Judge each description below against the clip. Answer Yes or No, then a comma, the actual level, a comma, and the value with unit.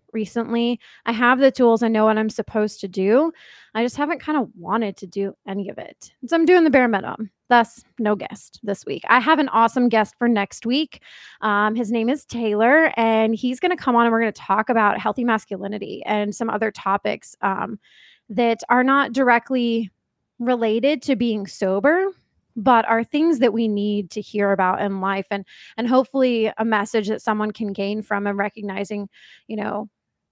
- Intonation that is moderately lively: Yes, average, 3.0 semitones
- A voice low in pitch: No, high, 225 Hz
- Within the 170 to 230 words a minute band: Yes, average, 195 wpm